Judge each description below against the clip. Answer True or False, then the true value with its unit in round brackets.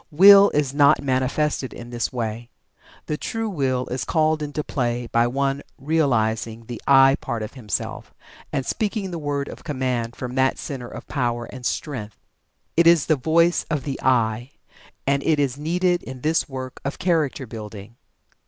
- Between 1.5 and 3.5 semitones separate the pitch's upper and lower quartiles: False (4.1 semitones)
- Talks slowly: False (170 wpm)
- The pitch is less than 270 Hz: True (135 Hz)